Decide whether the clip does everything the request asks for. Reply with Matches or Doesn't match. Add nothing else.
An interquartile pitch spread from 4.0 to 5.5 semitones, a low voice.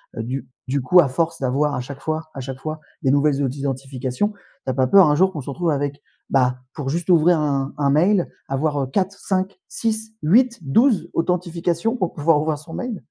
Doesn't match